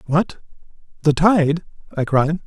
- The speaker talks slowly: Yes, slow, 120 wpm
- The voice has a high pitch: No, medium, 160 Hz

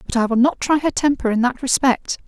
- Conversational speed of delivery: No, fast, 265 wpm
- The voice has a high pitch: Yes, very high, 260 Hz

